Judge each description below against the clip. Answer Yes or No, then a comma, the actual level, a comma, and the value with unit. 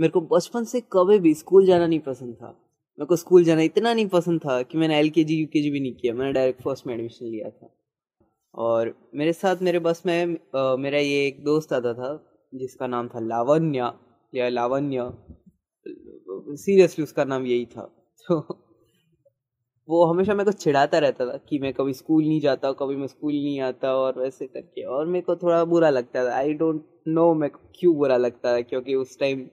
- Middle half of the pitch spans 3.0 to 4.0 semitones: No, average, 4.9 semitones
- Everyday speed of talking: No, fast, 195 wpm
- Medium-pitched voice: Yes, medium, 150 Hz